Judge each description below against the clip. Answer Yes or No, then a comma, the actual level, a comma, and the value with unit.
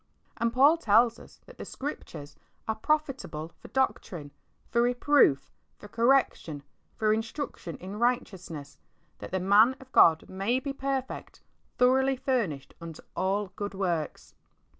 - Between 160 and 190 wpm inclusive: No, slow, 135 wpm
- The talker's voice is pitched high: Yes, high, 220 Hz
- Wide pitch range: Yes, wide, 6.5 semitones